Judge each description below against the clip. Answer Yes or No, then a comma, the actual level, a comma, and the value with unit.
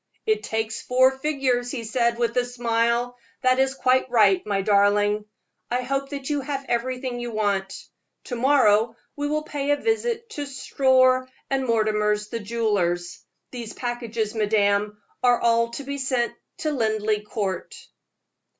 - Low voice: No, high, 240 Hz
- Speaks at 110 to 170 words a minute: Yes, average, 150 wpm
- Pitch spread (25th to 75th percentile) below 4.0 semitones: Yes, average, 3.6 semitones